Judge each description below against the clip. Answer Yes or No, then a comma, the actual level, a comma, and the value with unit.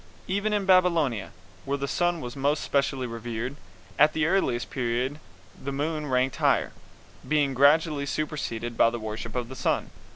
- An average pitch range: Yes, average, 4.1 semitones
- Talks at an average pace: Yes, average, 160 wpm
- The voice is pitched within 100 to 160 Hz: Yes, medium, 140 Hz